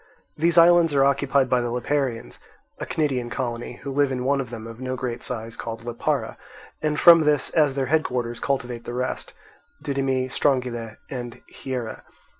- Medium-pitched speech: No, low, 130 Hz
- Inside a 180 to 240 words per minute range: No, average, 170 wpm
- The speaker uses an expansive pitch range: No, average, 2.8 semitones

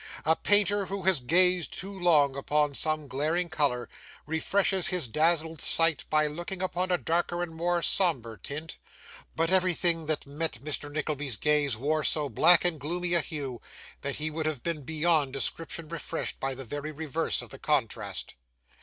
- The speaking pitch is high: No, medium, 160 Hz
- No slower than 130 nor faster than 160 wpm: No, average, 170 wpm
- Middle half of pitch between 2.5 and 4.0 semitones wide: Yes, average, 3.1 semitones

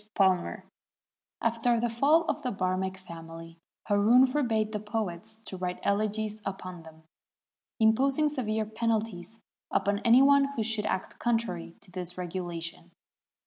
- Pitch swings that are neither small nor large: Yes, average, 4.1 semitones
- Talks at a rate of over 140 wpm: No, slow, 135 wpm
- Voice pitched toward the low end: No, high, 215 Hz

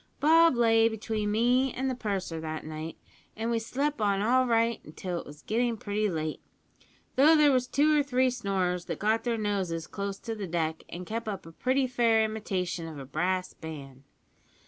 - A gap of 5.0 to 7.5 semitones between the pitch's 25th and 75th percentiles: Yes, wide, 5.5 semitones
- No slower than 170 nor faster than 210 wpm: Yes, average, 190 wpm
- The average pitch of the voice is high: Yes, high, 215 Hz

